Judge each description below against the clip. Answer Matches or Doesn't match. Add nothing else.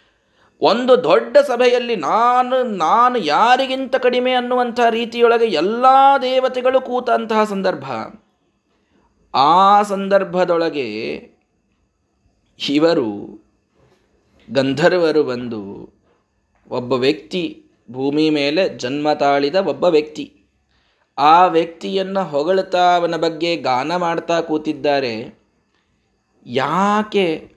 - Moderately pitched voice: Matches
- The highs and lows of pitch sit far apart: Matches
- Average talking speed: Matches